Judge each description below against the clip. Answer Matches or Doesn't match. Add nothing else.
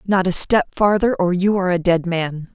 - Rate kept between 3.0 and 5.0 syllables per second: Matches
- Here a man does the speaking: Doesn't match